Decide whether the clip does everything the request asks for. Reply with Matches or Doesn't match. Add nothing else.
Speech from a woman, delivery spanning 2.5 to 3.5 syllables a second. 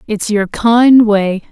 Matches